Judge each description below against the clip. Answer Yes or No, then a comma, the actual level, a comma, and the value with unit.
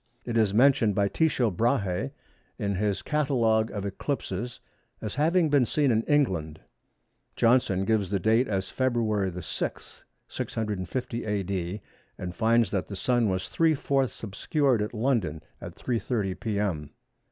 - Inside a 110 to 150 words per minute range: Yes, average, 140 wpm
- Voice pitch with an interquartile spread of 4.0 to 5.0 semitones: Yes, average, 4.4 semitones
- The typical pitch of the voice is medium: No, low, 110 Hz